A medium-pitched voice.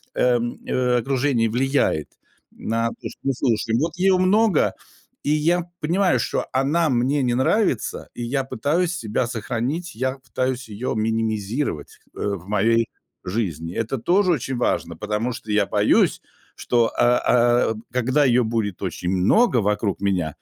No: low, 120 Hz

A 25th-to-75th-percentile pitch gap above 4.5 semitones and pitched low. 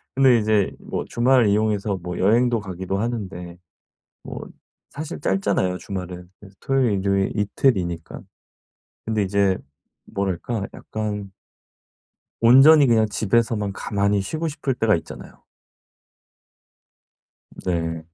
No: average, 3.6 semitones; low, 105 Hz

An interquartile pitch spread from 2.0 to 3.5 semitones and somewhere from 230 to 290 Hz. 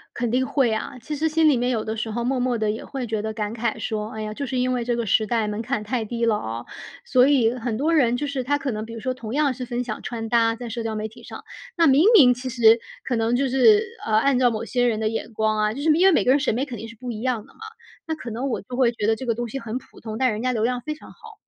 Yes: average, 2.8 semitones; high, 240 Hz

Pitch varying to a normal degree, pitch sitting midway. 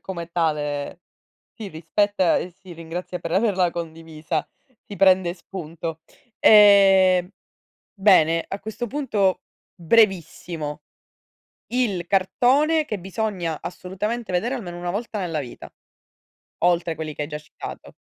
Yes: average, 3.7 semitones; medium, 180 Hz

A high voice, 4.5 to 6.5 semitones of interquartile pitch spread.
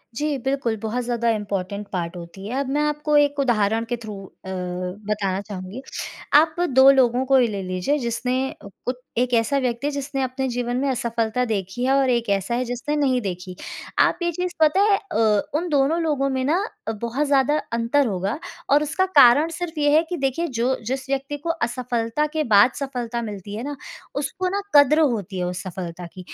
Yes: very high, 250 Hz; average, 5.1 semitones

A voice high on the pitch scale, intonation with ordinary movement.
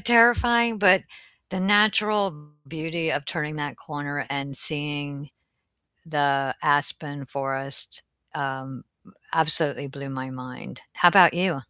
No: medium, 145 Hz; average, 4.3 semitones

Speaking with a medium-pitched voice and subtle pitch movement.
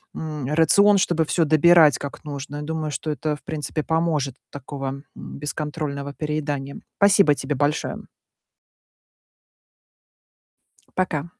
Yes: medium, 150 Hz; narrow, 2.1 semitones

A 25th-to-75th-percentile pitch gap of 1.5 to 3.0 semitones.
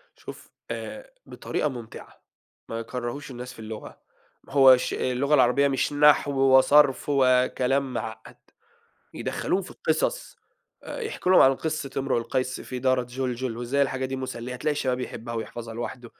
Yes: narrow, 2.4 semitones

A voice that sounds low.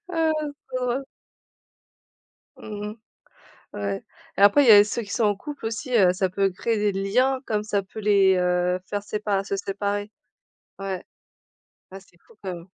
No: high, 205 Hz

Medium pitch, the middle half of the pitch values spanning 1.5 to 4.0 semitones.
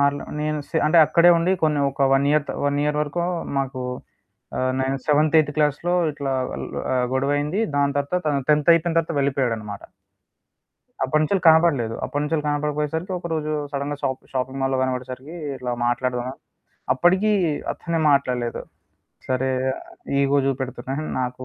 Yes: medium, 145 Hz; average, 2.8 semitones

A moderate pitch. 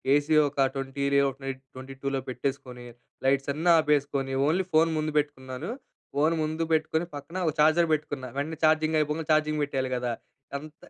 Yes: medium, 145 Hz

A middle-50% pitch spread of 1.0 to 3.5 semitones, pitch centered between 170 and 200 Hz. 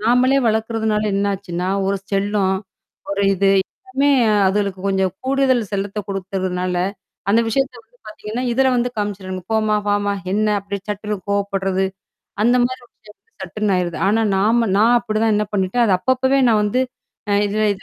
No: average, 2.8 semitones; high, 210 Hz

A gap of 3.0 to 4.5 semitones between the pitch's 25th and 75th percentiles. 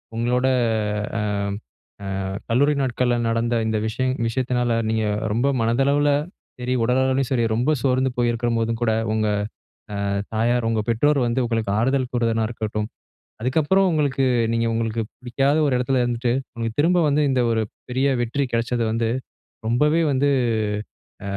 No: narrow, 2.6 semitones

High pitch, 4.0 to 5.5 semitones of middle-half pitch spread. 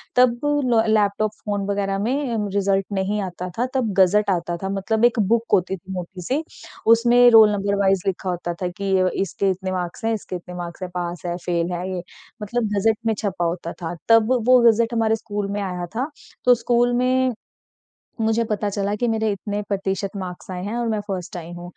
No: high, 200 Hz; average, 3.5 semitones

